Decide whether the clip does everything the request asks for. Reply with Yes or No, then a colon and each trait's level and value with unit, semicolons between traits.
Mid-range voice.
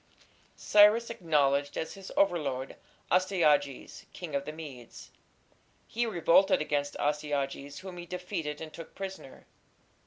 Yes: medium, 160 Hz